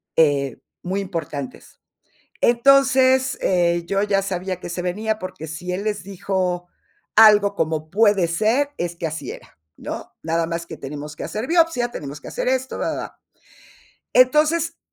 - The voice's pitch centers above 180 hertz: Yes, high, 190 Hz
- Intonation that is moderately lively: No, wide, 5.9 semitones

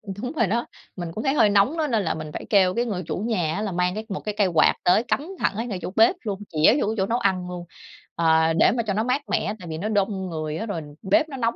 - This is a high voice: Yes, high, 200 Hz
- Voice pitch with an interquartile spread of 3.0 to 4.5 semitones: Yes, average, 4.2 semitones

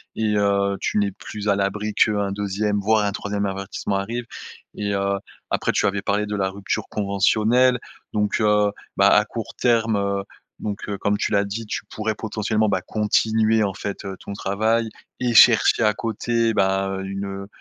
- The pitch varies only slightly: Yes, narrow, 1.6 semitones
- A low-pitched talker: Yes, low, 105 Hz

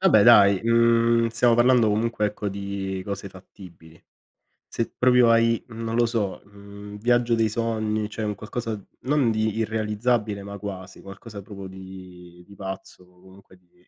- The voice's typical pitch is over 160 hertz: No, low, 105 Hz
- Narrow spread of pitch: No, average, 3.0 semitones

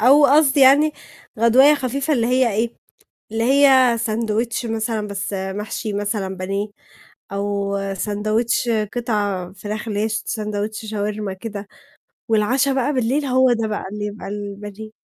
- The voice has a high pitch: Yes, high, 220 Hz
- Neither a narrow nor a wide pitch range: Yes, average, 3.4 semitones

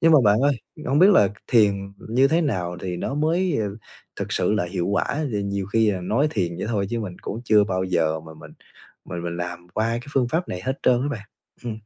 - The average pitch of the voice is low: Yes, low, 105 Hz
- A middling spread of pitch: No, wide, 6.4 semitones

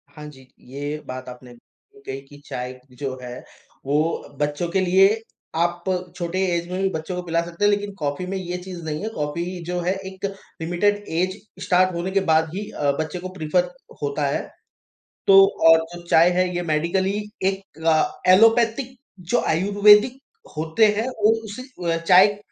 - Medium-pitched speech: Yes, medium, 175 Hz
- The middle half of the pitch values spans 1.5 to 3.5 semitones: No, average, 3.9 semitones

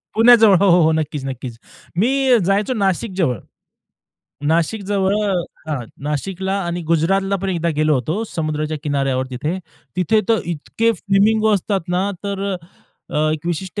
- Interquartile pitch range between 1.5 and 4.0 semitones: No, average, 4.6 semitones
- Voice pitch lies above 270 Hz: No, medium, 185 Hz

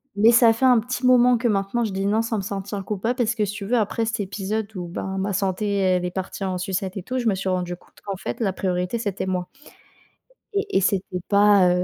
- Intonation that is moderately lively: Yes, average, 3.1 semitones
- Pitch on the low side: No, high, 200 Hz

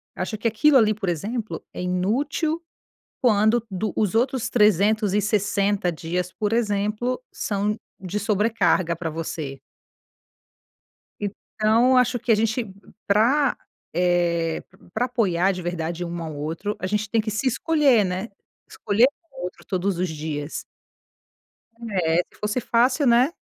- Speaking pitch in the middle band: No, high, 210 Hz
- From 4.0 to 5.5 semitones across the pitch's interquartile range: Yes, average, 4.4 semitones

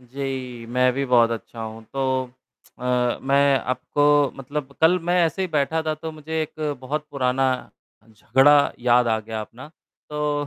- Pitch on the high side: No, low, 135 Hz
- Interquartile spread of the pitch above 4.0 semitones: No, average, 3.3 semitones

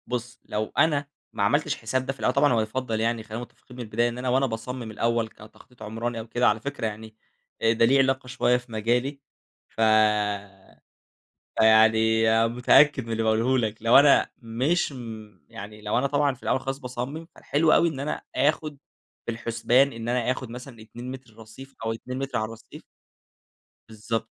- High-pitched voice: No, low, 120 Hz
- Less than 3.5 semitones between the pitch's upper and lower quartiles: Yes, average, 2.9 semitones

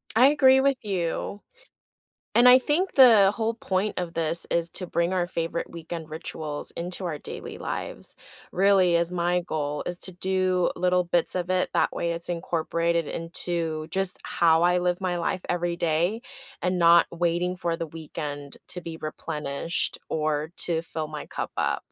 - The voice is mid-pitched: Yes, medium, 175 Hz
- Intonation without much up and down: Yes, narrow, 2.0 semitones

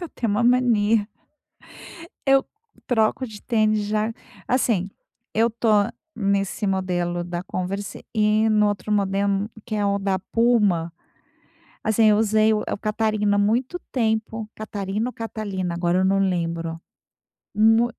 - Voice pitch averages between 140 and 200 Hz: No, high, 210 Hz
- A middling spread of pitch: No, narrow, 2.3 semitones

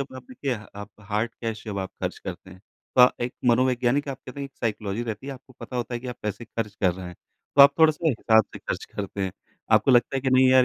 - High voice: No, low, 120 Hz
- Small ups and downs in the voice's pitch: No, average, 3.7 semitones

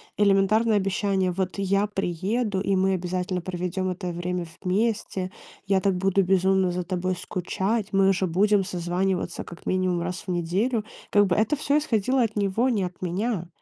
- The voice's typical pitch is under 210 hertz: Yes, high, 190 Hz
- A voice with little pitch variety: Yes, narrow, 2.1 semitones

